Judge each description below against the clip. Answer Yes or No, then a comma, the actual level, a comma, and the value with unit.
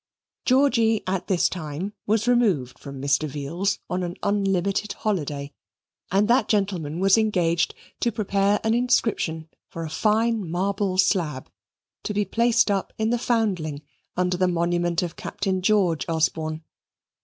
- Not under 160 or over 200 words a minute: No, average, 145 wpm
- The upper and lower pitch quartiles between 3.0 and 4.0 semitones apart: No, average, 4.5 semitones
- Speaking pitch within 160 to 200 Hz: Yes, high, 190 Hz